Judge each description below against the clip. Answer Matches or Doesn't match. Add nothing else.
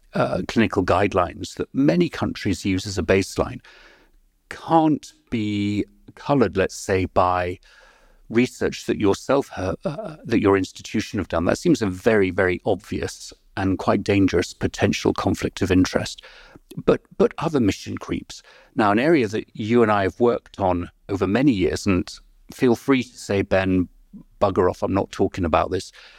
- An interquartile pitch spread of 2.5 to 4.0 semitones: Matches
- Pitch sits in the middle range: Doesn't match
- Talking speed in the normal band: Matches